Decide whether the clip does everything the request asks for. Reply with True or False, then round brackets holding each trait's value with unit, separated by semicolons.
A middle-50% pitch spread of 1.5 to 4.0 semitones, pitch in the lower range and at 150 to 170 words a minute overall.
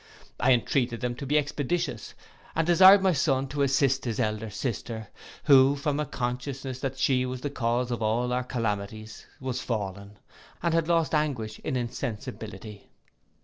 True (3.6 semitones; 125 Hz; 160 wpm)